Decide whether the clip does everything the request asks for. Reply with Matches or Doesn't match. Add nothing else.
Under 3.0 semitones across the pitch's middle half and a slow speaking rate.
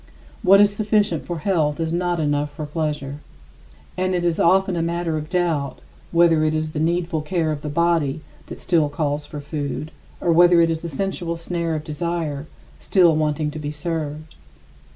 Doesn't match